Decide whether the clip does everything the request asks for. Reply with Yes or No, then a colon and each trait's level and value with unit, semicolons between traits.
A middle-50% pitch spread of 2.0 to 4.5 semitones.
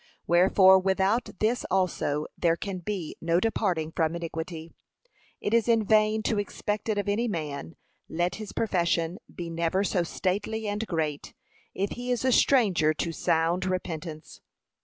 Yes: average, 4.2 semitones